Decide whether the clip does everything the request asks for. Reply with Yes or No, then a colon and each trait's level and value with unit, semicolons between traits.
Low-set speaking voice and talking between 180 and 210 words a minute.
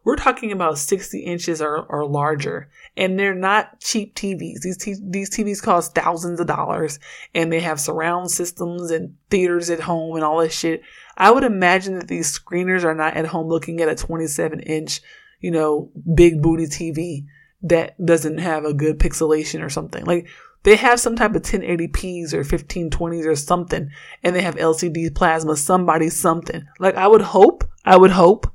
No: medium, 170 Hz; average, 185 wpm